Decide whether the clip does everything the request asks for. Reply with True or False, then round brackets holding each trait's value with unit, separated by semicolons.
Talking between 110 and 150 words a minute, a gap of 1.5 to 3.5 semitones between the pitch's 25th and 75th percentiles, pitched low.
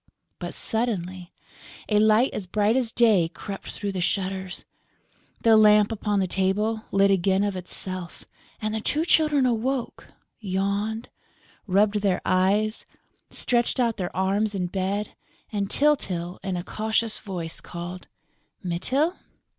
False (135 wpm; 2.9 semitones; 205 Hz)